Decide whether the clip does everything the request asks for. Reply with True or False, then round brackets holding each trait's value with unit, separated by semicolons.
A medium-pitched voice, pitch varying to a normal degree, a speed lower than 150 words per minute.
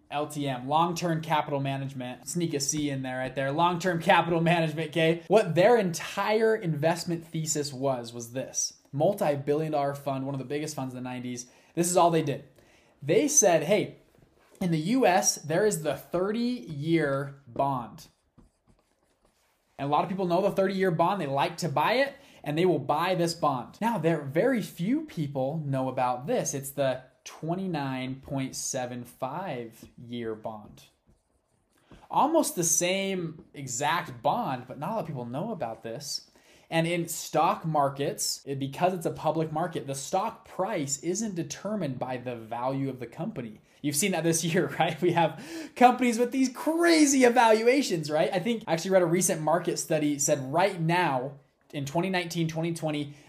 False (160 Hz; 4.6 semitones; 165 wpm)